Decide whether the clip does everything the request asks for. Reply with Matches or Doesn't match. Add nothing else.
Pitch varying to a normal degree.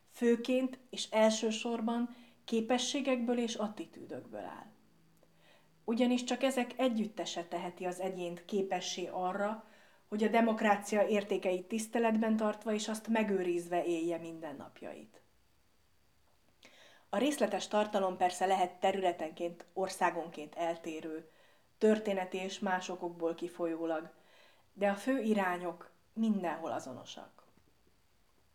Matches